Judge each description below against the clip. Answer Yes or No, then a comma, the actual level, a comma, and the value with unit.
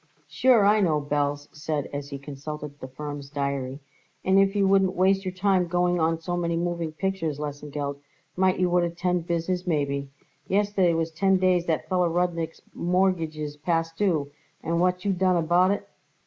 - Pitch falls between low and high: Yes, medium, 170 Hz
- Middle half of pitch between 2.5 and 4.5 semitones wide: Yes, average, 3.7 semitones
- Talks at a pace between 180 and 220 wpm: Yes, average, 185 wpm